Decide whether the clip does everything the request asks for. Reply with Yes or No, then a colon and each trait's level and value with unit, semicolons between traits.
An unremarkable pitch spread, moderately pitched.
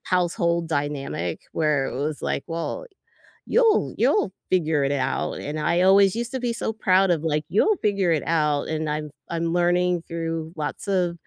Yes: average, 3.6 semitones; medium, 170 Hz